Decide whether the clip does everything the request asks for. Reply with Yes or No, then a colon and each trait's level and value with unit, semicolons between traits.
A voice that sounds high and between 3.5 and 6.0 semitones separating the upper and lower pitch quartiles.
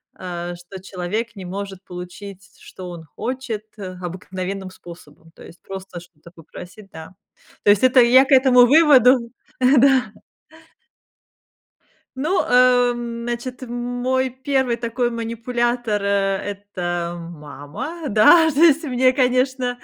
Yes: high, 230 Hz; wide, 5.5 semitones